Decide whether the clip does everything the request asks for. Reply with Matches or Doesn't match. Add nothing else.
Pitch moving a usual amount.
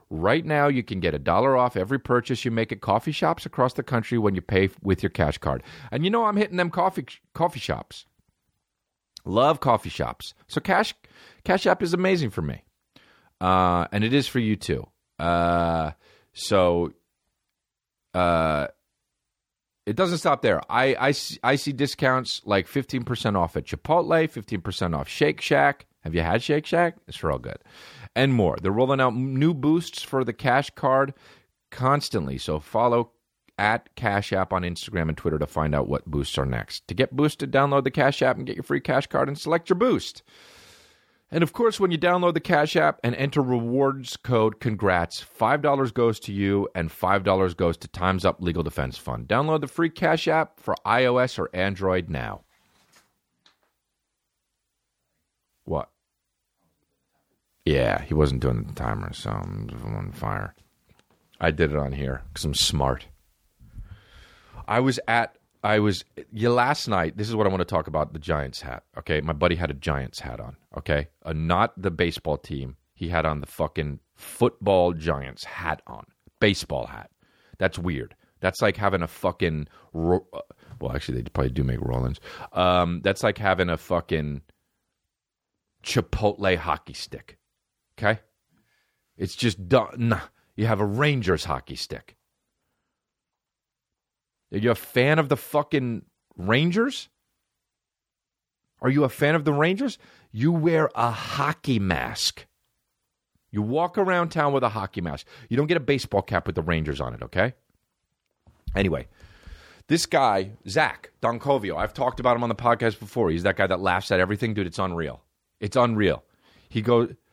Doesn't match